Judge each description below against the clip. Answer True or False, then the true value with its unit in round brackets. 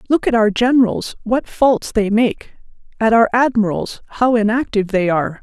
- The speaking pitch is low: False (225 Hz)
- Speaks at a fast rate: False (165 wpm)